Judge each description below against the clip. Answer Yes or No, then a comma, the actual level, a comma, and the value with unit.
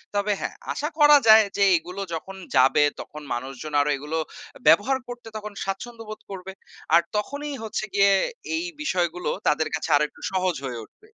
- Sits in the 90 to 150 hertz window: No, high, 195 Hz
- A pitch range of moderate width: No, wide, 6.0 semitones